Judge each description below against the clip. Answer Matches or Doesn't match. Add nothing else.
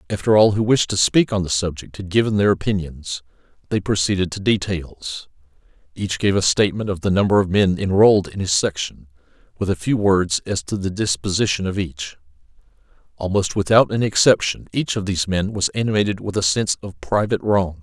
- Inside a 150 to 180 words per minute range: Doesn't match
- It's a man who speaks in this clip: Matches